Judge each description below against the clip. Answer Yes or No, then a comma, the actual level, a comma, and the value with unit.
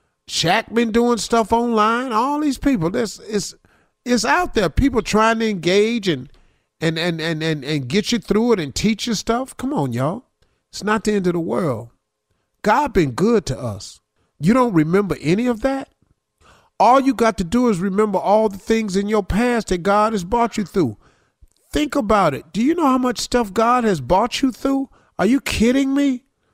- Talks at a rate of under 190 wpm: No, average, 200 wpm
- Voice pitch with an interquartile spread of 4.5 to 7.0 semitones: Yes, average, 5.1 semitones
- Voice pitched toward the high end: Yes, high, 215 Hz